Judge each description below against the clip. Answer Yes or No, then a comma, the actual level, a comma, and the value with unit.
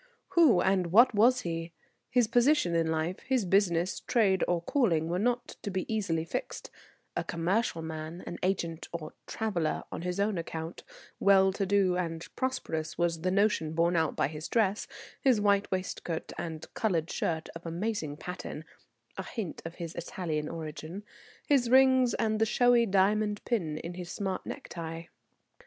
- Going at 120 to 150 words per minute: No, average, 165 wpm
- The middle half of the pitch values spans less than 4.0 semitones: No, average, 4.5 semitones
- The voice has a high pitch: No, medium, 180 Hz